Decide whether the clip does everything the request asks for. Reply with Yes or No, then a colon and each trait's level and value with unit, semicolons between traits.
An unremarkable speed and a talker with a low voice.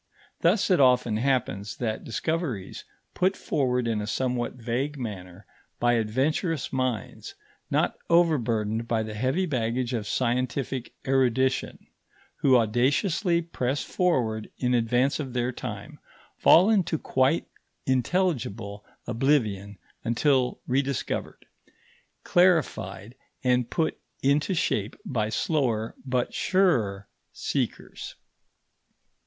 No: slow, 105 wpm; low, 125 Hz